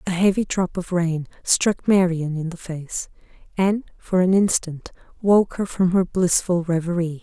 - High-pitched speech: No, medium, 180 Hz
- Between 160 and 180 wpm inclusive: Yes, average, 165 wpm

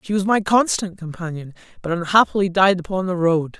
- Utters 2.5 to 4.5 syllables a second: No, 5.6 syllables/s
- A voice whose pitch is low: No, medium, 185 Hz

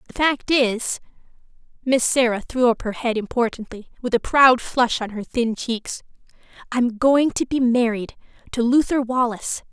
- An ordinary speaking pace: Yes, average, 150 wpm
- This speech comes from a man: No, female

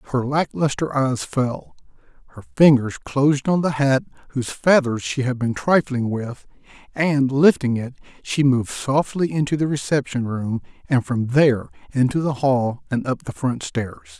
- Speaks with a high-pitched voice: No, low, 130 Hz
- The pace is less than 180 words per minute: Yes, average, 165 wpm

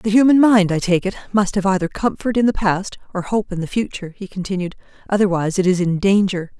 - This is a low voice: No, high, 195 Hz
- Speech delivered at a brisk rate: Yes, fast, 225 wpm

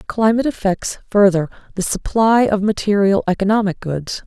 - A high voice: Yes, high, 200 Hz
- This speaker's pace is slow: Yes, slow, 125 wpm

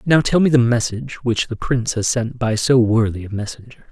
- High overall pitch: No, low, 120 Hz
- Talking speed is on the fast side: Yes, fast, 230 wpm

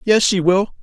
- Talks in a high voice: Yes, high, 195 Hz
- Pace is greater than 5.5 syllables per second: No, 4.4 syllables/s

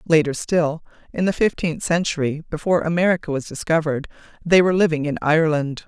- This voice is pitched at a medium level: Yes, medium, 160 Hz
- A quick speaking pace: No, average, 155 wpm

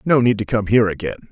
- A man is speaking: Yes, male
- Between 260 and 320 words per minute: Yes, fast, 275 wpm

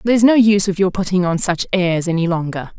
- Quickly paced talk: Yes, fast, 235 wpm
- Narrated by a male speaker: No, female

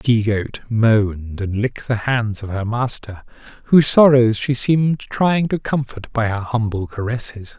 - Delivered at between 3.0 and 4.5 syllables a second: No, 4.8 syllables/s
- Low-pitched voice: Yes, low, 115 Hz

